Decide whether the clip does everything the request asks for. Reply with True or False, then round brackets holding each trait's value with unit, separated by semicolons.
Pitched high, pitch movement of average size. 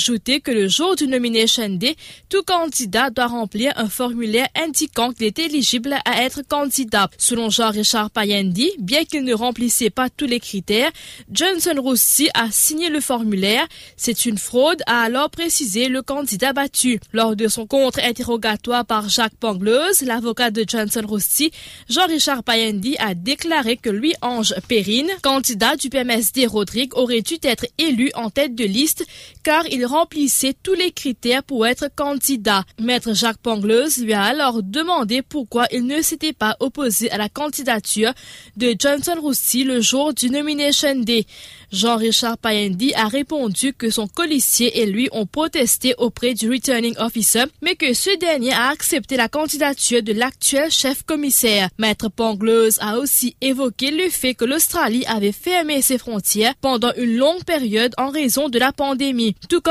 True (250 Hz; 3.9 semitones)